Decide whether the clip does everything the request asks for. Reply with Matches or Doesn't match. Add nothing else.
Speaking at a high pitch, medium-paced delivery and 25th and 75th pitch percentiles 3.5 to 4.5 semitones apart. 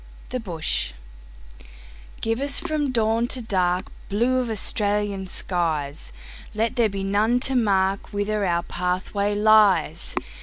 Doesn't match